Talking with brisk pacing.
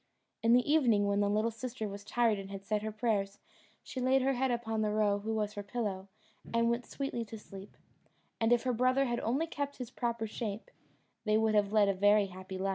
Yes: fast, 225 wpm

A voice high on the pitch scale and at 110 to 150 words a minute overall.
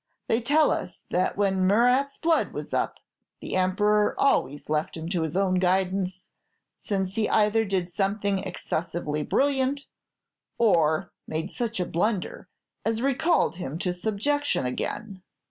Yes: high, 195 Hz; average, 140 wpm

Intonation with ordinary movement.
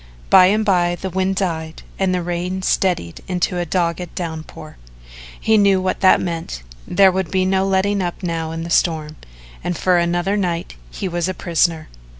No: narrow, 2.1 semitones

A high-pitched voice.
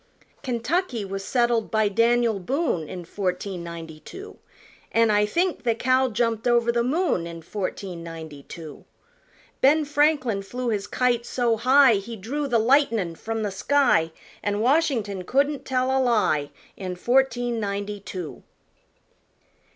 Yes: high, 230 Hz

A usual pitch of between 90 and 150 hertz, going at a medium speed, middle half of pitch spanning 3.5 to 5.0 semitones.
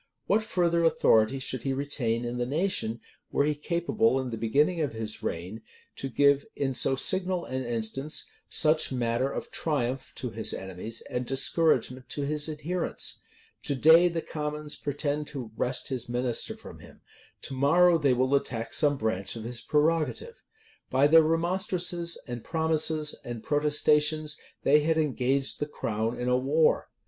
Yes: medium, 140 Hz; average, 160 wpm; average, 4.4 semitones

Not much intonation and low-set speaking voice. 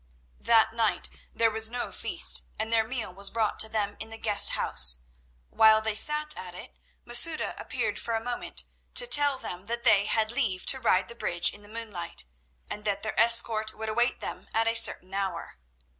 No: narrow, 2.3 semitones; high, 220 Hz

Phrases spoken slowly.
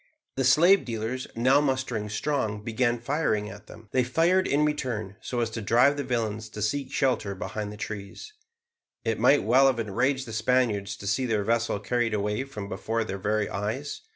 No: average, 185 wpm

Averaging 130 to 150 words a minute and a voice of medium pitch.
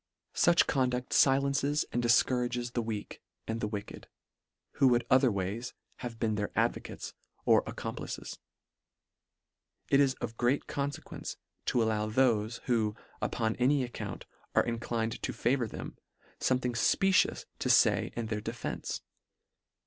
No: average, 140 wpm; low, 120 Hz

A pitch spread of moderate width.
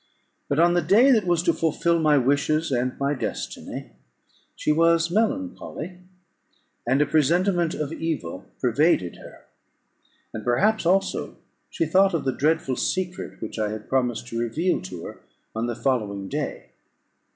No: wide, 6.1 semitones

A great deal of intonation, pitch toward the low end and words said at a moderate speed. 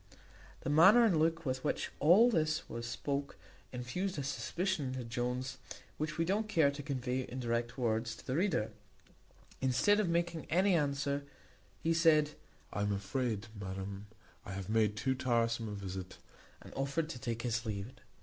Yes: wide, 5.8 semitones; low, 130 Hz; average, 170 wpm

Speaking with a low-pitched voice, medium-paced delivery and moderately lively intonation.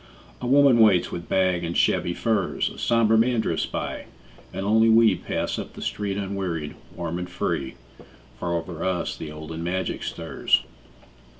Yes: very low, 95 Hz; average, 165 wpm; average, 4.6 semitones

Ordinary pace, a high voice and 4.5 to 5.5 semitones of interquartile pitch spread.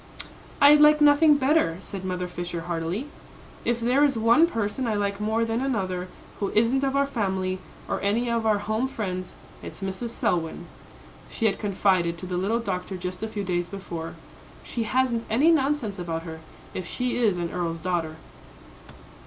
Yes: average, 175 wpm; high, 205 Hz; average, 5.1 semitones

